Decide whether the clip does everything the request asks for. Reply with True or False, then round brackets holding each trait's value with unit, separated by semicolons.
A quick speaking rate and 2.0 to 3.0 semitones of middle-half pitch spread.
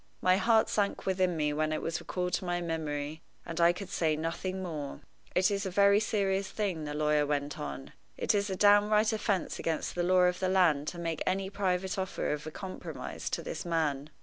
False (210 wpm; 3.7 semitones)